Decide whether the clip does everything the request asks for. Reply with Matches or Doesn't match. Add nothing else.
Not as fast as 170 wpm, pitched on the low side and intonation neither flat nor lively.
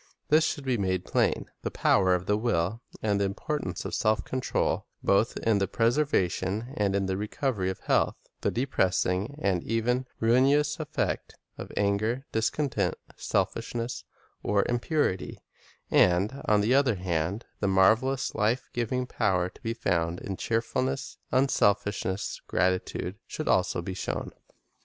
Matches